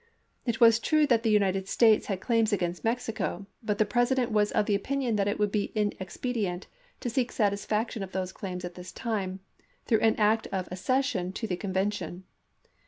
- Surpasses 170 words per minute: Yes, average, 185 wpm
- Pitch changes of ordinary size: Yes, average, 3.3 semitones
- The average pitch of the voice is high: Yes, high, 210 Hz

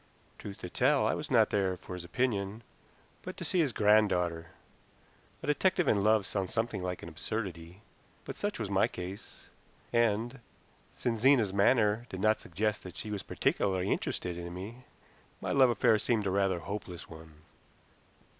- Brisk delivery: No, average, 165 wpm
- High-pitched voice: No, low, 100 Hz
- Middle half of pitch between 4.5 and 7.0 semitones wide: No, average, 3.7 semitones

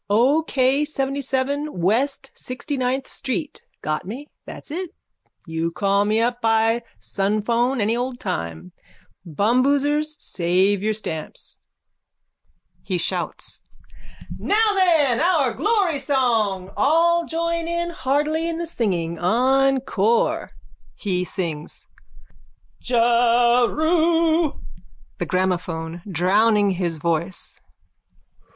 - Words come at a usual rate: No, slow, 95 wpm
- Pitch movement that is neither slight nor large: No, wide, 7.1 semitones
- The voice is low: No, high, 245 Hz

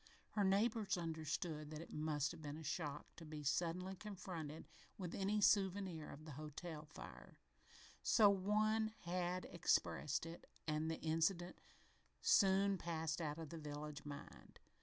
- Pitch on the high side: No, medium, 165 Hz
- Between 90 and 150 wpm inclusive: Yes, average, 145 wpm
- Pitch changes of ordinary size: Yes, average, 3.8 semitones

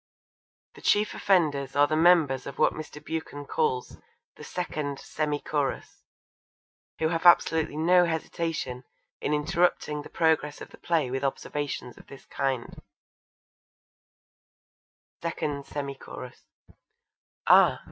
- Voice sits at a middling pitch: Yes, medium, 150 Hz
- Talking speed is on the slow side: Yes, slow, 120 wpm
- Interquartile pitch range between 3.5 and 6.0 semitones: No, average, 2.9 semitones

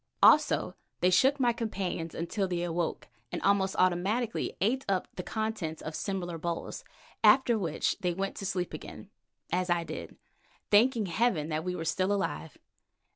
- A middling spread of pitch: Yes, average, 3.9 semitones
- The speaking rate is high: No, average, 165 wpm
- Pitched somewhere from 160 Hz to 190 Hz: Yes, medium, 185 Hz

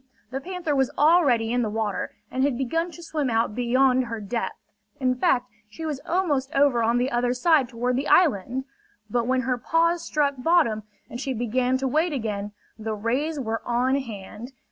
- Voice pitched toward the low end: No, very high, 255 Hz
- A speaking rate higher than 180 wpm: Yes, average, 190 wpm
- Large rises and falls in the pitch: No, average, 3.5 semitones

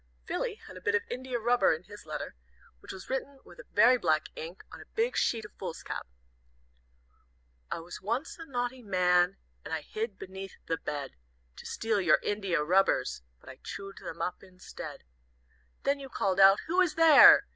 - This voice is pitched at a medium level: No, high, 200 Hz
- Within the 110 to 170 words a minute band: No, average, 180 wpm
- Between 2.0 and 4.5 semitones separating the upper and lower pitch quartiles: No, wide, 5.4 semitones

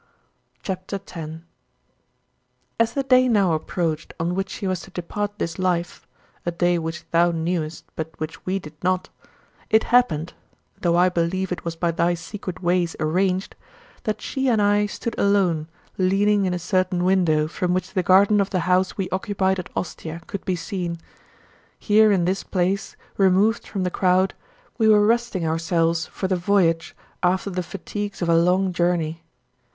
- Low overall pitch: No, medium, 185 Hz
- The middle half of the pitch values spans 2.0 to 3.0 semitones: Yes, narrow, 2.6 semitones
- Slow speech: No, average, 170 wpm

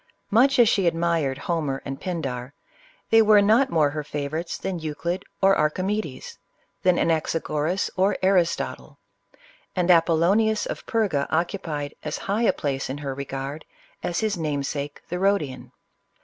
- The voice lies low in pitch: No, medium, 165 Hz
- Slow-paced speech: No, average, 145 wpm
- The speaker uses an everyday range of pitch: Yes, average, 5.0 semitones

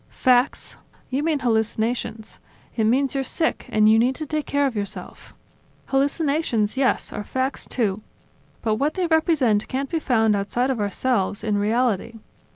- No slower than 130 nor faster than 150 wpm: No, average, 160 wpm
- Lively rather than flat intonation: No, average, 4.3 semitones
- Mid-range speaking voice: No, very high, 250 Hz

